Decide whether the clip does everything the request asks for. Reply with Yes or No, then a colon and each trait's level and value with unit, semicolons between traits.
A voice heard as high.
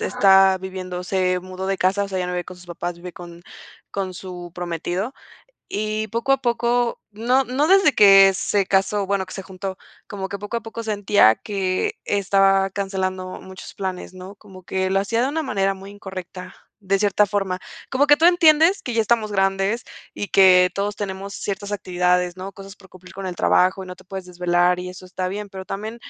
Yes: high, 195 Hz